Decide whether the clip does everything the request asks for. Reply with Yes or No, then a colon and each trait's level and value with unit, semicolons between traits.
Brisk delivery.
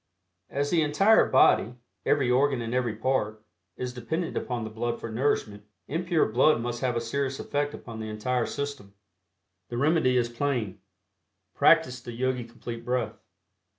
No: average, 155 wpm